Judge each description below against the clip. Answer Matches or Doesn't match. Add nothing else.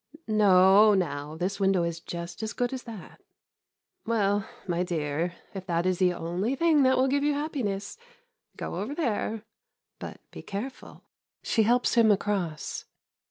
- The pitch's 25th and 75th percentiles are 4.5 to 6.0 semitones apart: Matches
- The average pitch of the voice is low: Doesn't match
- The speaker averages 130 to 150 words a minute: Doesn't match